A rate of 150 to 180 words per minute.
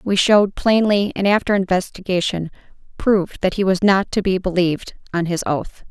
Yes: average, 175 wpm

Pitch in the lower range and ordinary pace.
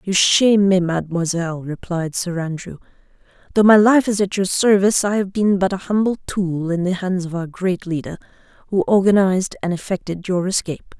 No: medium, 185 Hz; average, 185 wpm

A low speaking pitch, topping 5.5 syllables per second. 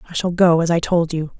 No: medium, 170 Hz; 6.2 syllables/s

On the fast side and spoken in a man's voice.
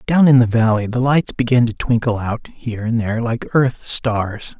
Yes: fast, 210 wpm; male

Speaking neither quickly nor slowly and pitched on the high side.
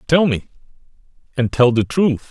No: average, 155 wpm; low, 130 Hz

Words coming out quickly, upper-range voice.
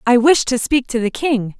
Yes: fast, 265 wpm; high, 245 Hz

